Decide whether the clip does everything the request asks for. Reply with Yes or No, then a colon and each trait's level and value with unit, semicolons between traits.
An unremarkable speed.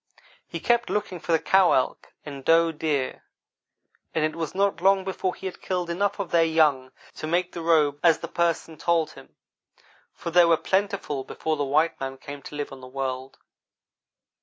Yes: average, 190 wpm